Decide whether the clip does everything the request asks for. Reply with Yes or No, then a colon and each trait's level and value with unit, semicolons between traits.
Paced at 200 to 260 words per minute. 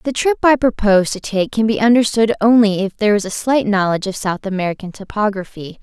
Yes: fast, 205 wpm